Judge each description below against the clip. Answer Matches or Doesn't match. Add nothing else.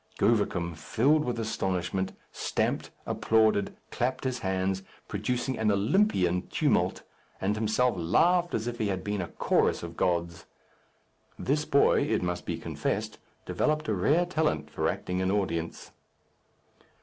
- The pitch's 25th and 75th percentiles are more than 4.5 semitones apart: Matches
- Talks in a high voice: Doesn't match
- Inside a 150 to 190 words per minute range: Doesn't match